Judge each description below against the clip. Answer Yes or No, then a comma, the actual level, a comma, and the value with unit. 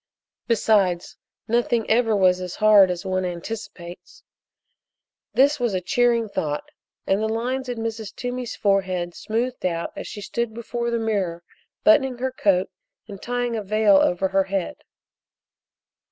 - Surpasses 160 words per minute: No, average, 145 wpm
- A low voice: No, high, 215 Hz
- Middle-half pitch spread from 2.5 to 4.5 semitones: Yes, average, 4.1 semitones